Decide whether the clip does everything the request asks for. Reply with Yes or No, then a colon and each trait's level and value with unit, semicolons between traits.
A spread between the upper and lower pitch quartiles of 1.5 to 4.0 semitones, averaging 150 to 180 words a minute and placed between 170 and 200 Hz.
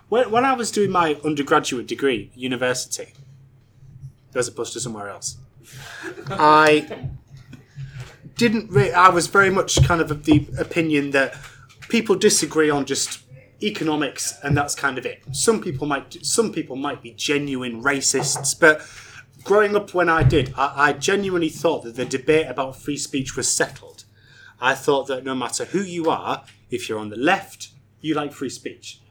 No: average, 3.6 semitones; average, 170 wpm; medium, 140 Hz